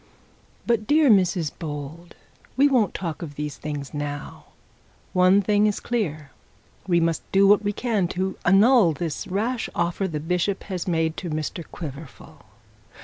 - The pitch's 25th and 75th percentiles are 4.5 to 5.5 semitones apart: Yes, average, 4.8 semitones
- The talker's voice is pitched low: No, medium, 175 Hz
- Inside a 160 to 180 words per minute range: No, average, 145 wpm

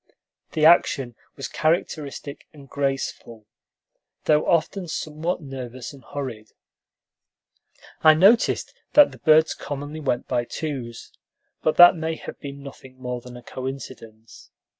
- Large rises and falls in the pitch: No, average, 3.5 semitones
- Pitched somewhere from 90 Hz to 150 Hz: Yes, medium, 140 Hz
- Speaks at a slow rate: Yes, slow, 125 wpm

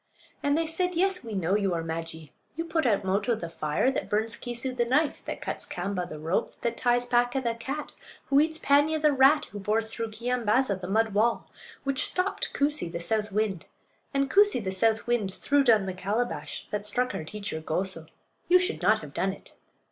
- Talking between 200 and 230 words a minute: Yes, fast, 205 wpm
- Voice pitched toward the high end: Yes, high, 230 Hz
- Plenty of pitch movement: Yes, wide, 6.0 semitones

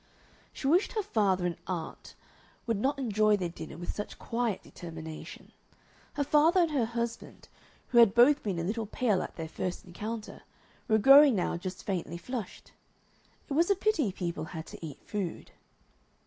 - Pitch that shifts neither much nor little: No, wide, 6.8 semitones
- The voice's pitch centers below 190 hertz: No, high, 215 Hz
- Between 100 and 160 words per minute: No, average, 170 wpm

